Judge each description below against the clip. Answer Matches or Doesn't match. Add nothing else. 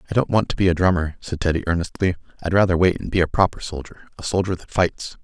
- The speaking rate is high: Matches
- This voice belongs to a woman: Doesn't match